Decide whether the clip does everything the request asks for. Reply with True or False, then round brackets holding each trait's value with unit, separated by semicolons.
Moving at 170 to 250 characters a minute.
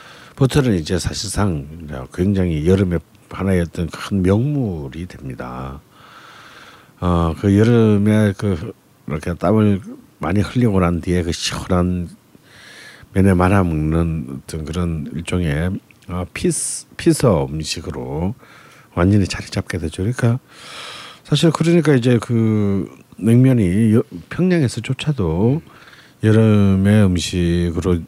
True (230 characters per minute)